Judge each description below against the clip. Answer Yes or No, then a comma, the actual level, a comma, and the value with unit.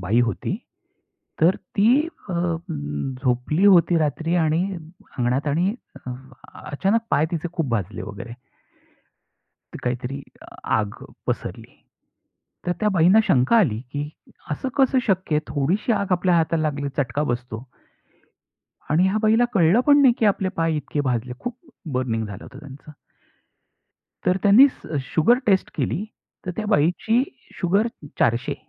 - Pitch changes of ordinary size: No, wide, 7.2 semitones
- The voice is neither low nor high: Yes, medium, 160 Hz